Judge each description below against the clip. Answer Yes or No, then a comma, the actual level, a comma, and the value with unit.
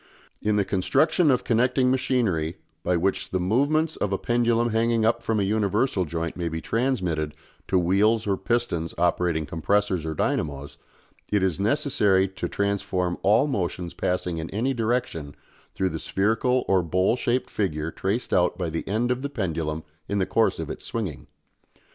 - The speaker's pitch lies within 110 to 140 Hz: No, low, 100 Hz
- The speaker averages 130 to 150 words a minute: No, average, 170 wpm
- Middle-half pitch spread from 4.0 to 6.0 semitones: Yes, wide, 5.4 semitones